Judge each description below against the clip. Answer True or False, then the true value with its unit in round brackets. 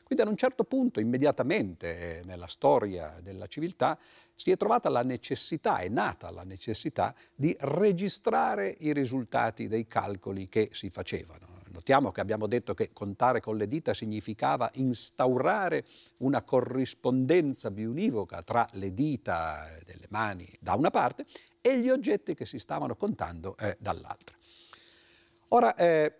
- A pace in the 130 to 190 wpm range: True (140 wpm)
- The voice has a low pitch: True (115 Hz)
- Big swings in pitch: True (6.3 semitones)